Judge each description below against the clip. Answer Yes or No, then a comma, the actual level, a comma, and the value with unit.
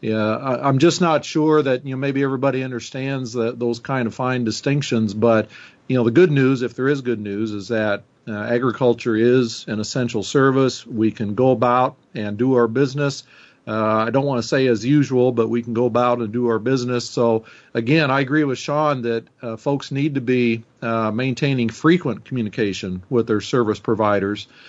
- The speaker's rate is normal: Yes, average, 195 wpm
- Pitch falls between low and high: No, low, 125 Hz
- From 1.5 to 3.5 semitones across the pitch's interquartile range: Yes, average, 3.1 semitones